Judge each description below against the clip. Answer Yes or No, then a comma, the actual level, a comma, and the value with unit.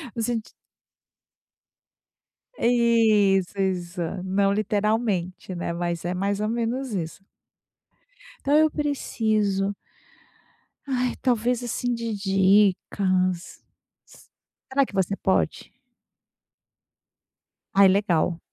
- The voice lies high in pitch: Yes, high, 200 Hz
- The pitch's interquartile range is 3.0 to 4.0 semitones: Yes, average, 3.7 semitones